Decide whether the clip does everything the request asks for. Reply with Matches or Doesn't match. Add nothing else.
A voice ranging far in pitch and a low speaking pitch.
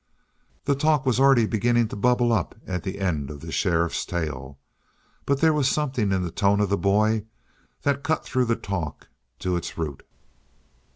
Matches